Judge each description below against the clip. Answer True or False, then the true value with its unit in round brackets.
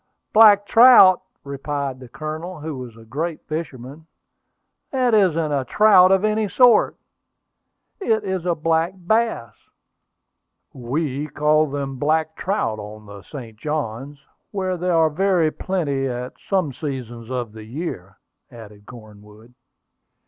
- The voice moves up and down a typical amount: False (6.8 semitones)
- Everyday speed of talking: False (130 wpm)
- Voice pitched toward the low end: False (150 Hz)